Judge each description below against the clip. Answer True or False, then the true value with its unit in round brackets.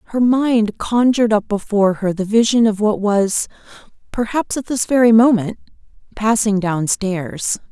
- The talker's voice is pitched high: True (215 Hz)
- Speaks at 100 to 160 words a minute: True (140 wpm)